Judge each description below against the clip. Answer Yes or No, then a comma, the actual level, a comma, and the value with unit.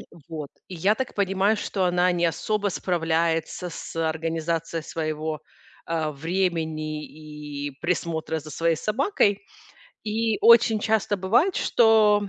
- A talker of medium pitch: Yes, medium, 170 Hz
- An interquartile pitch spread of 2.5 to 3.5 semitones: No, average, 4.4 semitones